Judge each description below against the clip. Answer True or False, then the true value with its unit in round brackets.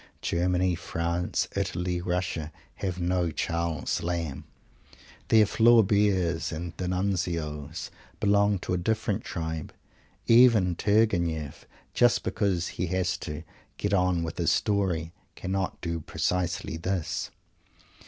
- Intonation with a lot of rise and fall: False (2.7 semitones)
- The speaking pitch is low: True (90 Hz)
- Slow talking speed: True (110 wpm)